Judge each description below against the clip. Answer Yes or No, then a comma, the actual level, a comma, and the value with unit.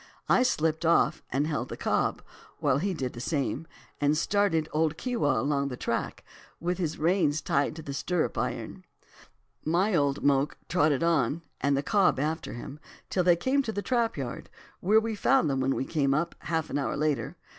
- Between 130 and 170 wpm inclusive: No, average, 190 wpm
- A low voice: No, medium, 155 Hz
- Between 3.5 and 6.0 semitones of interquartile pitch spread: Yes, average, 4.2 semitones